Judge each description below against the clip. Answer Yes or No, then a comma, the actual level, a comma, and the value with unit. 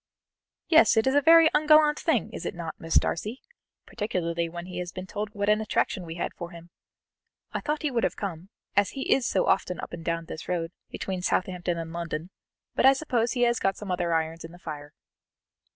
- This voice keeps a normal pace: No, fast, 215 wpm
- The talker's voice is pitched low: No, medium, 185 Hz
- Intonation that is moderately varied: No, wide, 5.9 semitones